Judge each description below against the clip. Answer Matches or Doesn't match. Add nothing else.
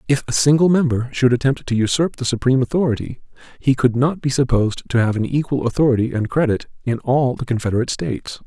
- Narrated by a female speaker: Doesn't match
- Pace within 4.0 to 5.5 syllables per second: Doesn't match